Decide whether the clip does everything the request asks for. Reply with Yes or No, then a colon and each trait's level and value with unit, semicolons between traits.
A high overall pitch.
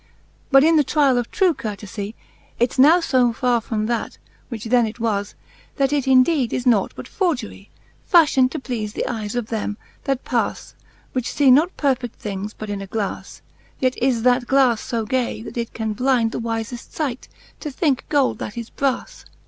Yes: high, 245 Hz